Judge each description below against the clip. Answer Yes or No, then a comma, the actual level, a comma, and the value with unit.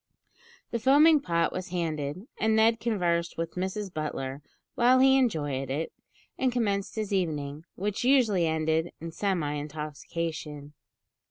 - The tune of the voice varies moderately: No, wide, 6.1 semitones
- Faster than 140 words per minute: No, slow, 135 wpm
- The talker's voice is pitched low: No, medium, 175 Hz